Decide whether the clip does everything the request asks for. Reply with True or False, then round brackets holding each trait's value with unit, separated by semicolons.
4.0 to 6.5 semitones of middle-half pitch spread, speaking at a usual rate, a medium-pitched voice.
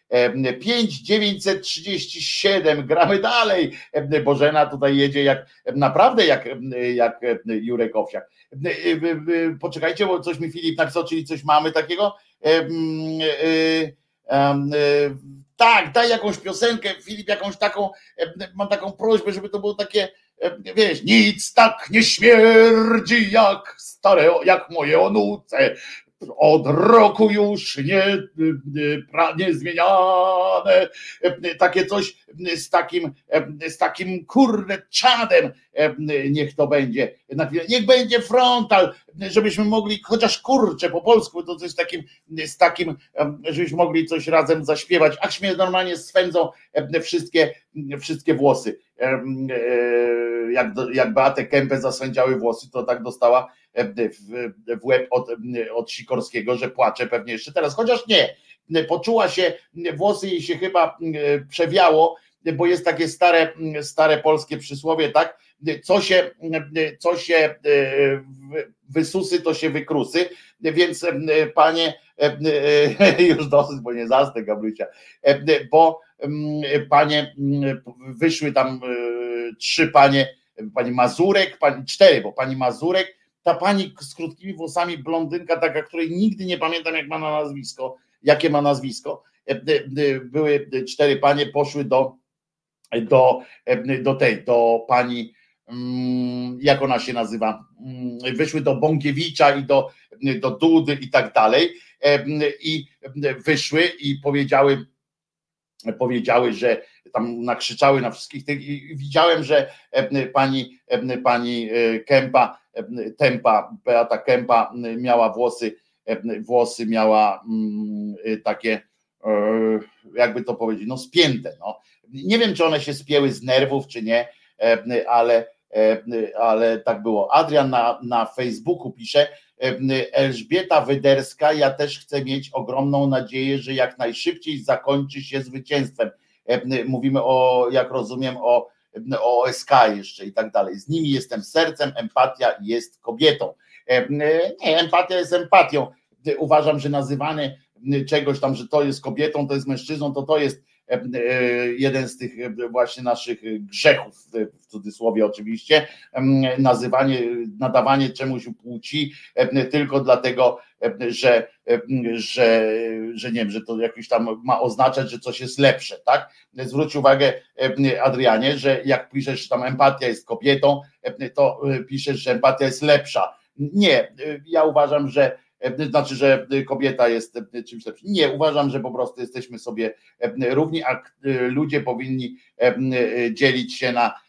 True (4.6 semitones; 125 wpm; 145 Hz)